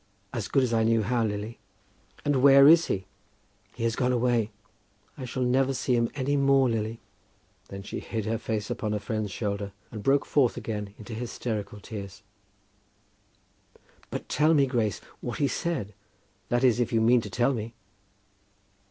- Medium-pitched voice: No, low, 115 Hz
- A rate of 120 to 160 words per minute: No, average, 170 wpm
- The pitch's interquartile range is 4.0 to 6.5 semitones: No, average, 3.3 semitones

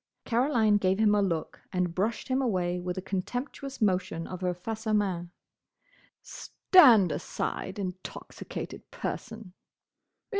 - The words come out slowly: Yes, slow, 125 wpm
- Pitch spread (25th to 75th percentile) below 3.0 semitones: No, average, 3.7 semitones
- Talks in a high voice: Yes, high, 195 Hz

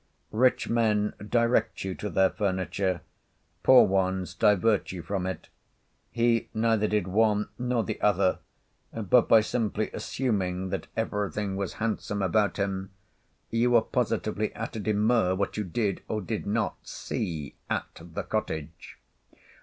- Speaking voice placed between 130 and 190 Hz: No, low, 105 Hz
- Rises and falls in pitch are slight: No, average, 3.1 semitones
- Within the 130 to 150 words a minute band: Yes, average, 140 wpm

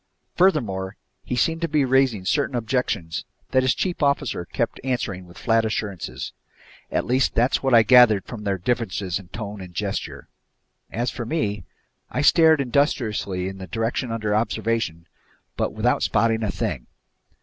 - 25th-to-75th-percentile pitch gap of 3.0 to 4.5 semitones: No, average, 5.1 semitones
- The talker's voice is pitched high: No, low, 115 Hz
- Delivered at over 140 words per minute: Yes, average, 160 wpm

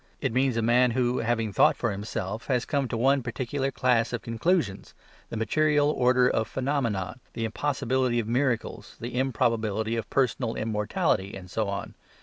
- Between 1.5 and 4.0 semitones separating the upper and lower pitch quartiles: Yes, average, 2.8 semitones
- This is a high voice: No, low, 120 Hz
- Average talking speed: Yes, average, 165 wpm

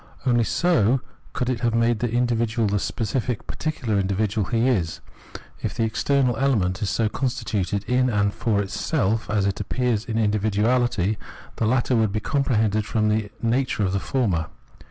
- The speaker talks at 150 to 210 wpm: Yes, average, 165 wpm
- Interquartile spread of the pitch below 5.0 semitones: Yes, average, 3.1 semitones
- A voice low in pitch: Yes, low, 110 Hz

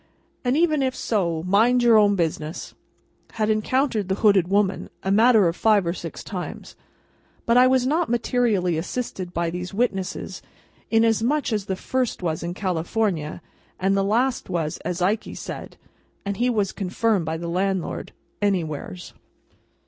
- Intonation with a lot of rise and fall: No, average, 4.7 semitones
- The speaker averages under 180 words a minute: Yes, average, 155 wpm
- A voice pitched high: Yes, high, 200 Hz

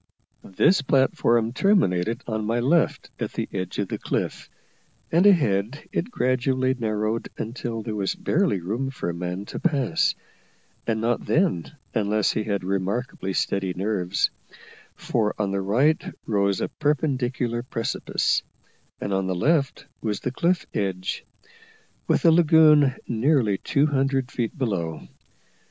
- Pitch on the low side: Yes, low, 115 Hz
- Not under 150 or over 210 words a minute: No, average, 140 wpm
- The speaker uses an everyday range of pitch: No, wide, 5.7 semitones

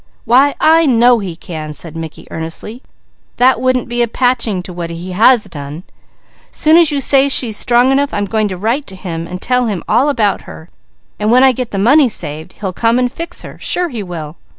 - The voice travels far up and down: Yes, wide, 6.3 semitones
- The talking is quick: Yes, fast, 220 wpm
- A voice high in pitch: Yes, high, 225 Hz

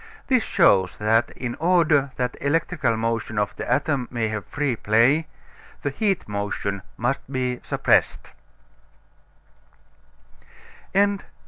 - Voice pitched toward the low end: Yes, low, 125 Hz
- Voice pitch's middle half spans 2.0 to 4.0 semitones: No, average, 4.9 semitones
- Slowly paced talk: Yes, slow, 110 wpm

